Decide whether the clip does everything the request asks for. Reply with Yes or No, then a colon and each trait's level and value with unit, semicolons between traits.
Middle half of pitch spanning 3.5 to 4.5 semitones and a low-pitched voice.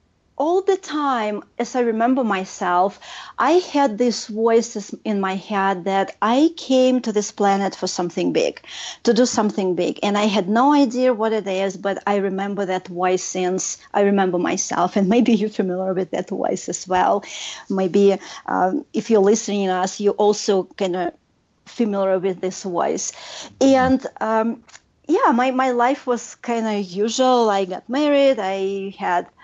No: average, 4.1 semitones; high, 210 Hz